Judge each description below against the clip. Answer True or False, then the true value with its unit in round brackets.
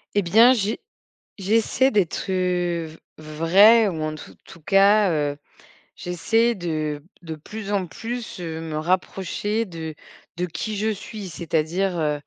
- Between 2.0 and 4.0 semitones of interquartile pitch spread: False (4.5 semitones)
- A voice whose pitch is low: False (180 Hz)